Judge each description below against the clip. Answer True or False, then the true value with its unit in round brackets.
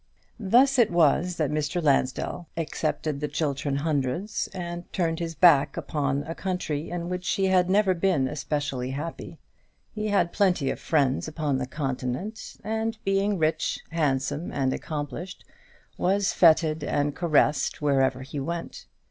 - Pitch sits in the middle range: True (160 Hz)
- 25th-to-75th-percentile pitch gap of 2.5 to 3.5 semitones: False (4.2 semitones)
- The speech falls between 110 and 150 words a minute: True (145 wpm)